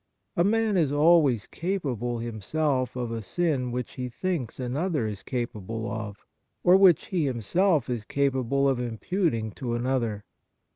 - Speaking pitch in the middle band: No, low, 130 Hz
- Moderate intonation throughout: No, wide, 5.8 semitones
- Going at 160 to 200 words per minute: No, average, 145 wpm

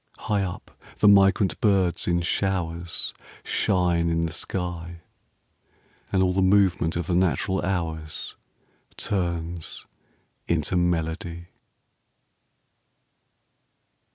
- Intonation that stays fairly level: Yes, narrow, 2.1 semitones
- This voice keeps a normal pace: No, slow, 95 wpm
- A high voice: No, very low, 85 Hz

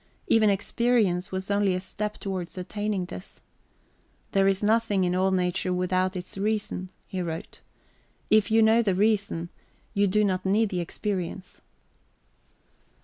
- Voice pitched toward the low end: No, high, 195 Hz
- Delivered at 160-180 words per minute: No, average, 145 wpm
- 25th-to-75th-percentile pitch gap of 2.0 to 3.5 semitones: Yes, narrow, 2.5 semitones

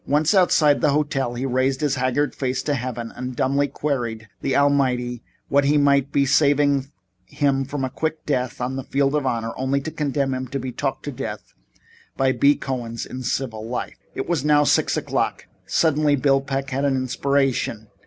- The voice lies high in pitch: No, low, 135 Hz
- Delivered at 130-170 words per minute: No, average, 185 wpm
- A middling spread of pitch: No, narrow, 2.0 semitones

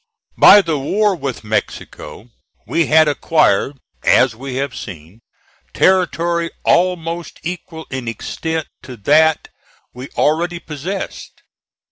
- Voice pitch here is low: No, medium, 155 Hz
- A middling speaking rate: No, slow, 110 wpm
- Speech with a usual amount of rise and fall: Yes, average, 4.7 semitones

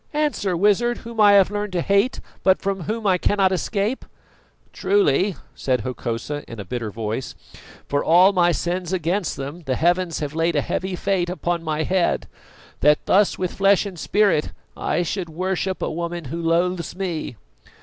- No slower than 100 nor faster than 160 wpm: No, average, 170 wpm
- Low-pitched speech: No, medium, 180 Hz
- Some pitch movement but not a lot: Yes, average, 3.7 semitones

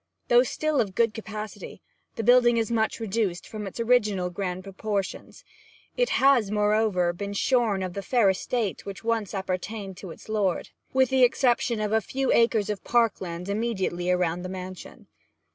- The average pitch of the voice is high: Yes, high, 210 Hz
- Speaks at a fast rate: No, average, 170 wpm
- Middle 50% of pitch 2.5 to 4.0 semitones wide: Yes, average, 3.6 semitones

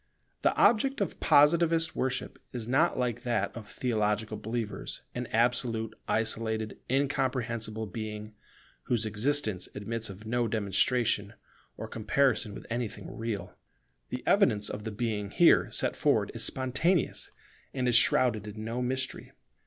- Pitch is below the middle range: Yes, low, 115 Hz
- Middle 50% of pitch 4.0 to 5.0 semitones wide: No, average, 3.1 semitones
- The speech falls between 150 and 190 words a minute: No, slow, 135 wpm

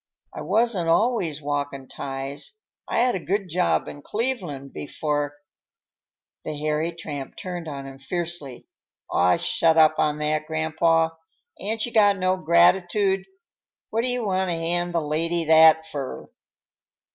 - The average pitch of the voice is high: No, medium, 165 Hz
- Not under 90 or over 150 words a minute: Yes, average, 145 wpm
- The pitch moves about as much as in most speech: Yes, average, 3.9 semitones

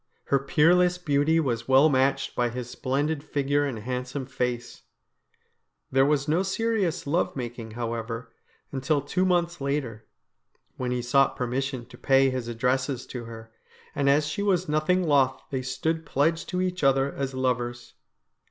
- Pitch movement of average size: Yes, average, 3.6 semitones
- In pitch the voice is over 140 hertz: No, low, 135 Hz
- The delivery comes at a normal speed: Yes, average, 155 wpm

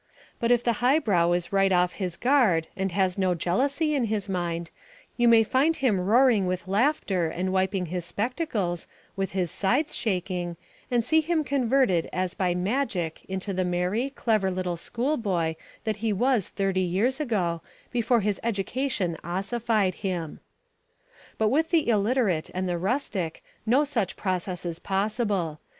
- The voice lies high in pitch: Yes, high, 195 Hz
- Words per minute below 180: Yes, average, 160 wpm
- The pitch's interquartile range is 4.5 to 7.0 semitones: Yes, average, 5.1 semitones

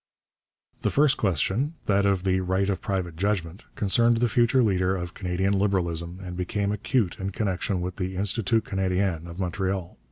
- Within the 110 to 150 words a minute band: No, average, 165 wpm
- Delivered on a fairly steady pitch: Yes, narrow, 2.3 semitones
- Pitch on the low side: Yes, very low, 95 Hz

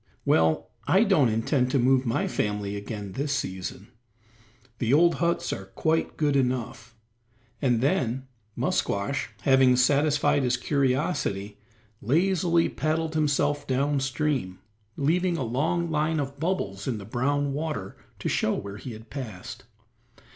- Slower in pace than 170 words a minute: Yes, slow, 135 wpm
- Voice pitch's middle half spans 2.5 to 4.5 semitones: No, average, 5.1 semitones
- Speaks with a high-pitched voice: No, low, 135 Hz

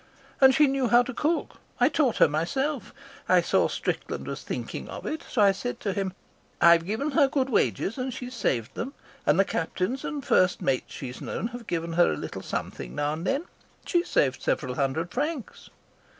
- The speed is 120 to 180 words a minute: No, average, 200 wpm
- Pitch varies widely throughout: Yes, wide, 8.3 semitones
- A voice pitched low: No, high, 230 Hz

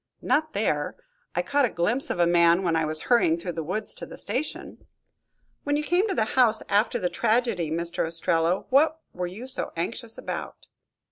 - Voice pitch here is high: Yes, high, 200 Hz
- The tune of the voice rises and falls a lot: Yes, wide, 7.1 semitones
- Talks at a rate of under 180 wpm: No, average, 195 wpm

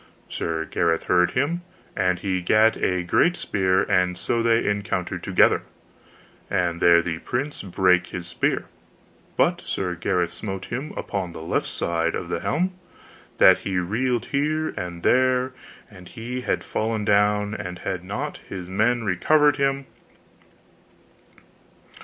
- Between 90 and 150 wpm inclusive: Yes, average, 140 wpm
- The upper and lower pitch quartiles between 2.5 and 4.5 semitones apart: No, wide, 5.4 semitones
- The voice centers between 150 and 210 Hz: No, very low, 95 Hz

